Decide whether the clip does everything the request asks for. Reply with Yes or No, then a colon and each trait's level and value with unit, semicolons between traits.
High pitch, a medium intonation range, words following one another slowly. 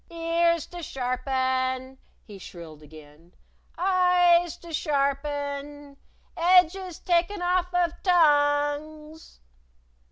Yes: very high, 300 Hz; average, 4.7 semitones; slow, 85 wpm